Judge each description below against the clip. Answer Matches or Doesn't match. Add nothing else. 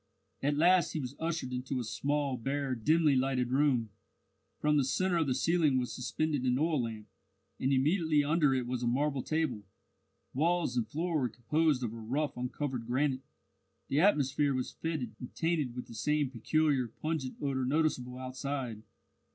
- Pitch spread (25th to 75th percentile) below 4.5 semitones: Matches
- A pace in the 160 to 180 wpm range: Matches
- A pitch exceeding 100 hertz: Matches